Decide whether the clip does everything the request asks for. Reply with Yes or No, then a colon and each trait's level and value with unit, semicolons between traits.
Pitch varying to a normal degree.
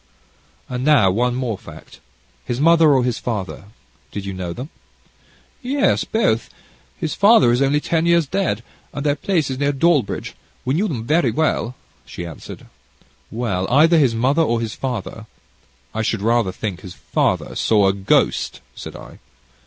No: wide, 5.8 semitones